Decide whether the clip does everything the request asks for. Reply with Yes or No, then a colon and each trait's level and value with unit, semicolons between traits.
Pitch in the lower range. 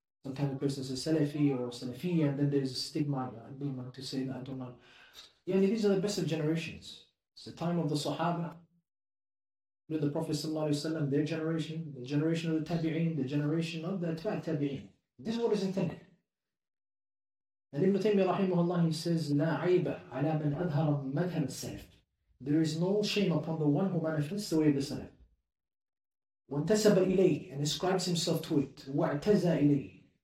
No: medium, 155 Hz